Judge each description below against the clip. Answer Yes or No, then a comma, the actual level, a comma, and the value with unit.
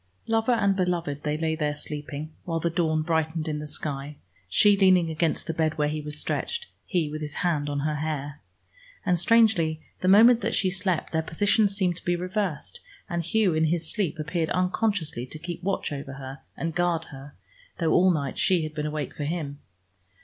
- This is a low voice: No, medium, 160 Hz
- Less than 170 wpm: No, average, 195 wpm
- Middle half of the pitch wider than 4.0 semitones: No, average, 3.3 semitones